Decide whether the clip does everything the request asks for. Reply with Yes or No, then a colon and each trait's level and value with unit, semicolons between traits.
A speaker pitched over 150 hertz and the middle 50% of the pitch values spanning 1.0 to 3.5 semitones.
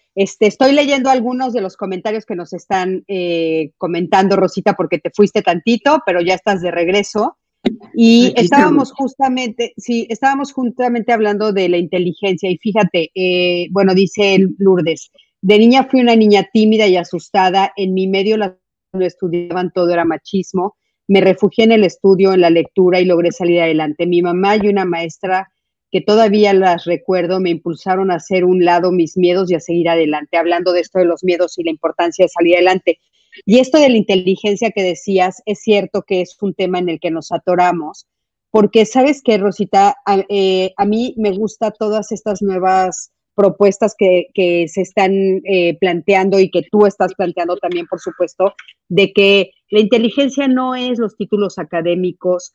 Yes: high, 190 Hz; average, 3.1 semitones